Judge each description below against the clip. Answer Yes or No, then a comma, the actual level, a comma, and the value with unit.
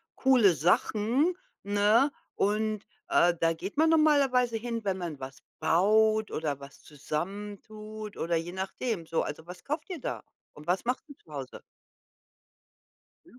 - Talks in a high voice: Yes, high, 205 Hz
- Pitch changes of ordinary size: No, wide, 6.0 semitones